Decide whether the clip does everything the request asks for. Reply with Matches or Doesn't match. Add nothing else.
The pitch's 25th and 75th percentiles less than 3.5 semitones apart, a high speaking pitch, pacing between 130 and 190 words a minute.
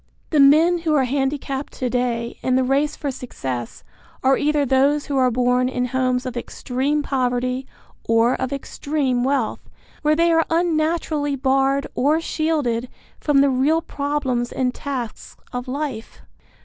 Matches